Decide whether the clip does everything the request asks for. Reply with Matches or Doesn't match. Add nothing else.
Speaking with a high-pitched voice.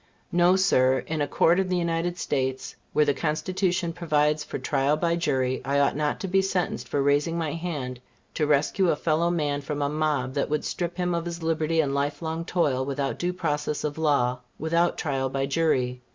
Doesn't match